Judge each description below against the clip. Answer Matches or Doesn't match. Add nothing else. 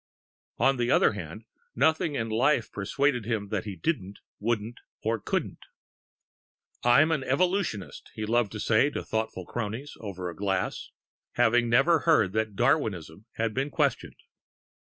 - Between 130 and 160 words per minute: Matches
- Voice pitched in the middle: Doesn't match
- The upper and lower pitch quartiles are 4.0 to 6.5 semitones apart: Matches